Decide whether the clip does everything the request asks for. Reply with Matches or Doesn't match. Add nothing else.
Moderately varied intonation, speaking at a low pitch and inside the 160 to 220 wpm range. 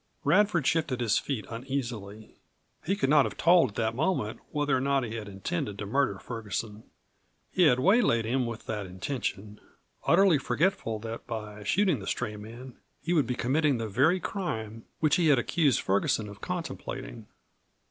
Doesn't match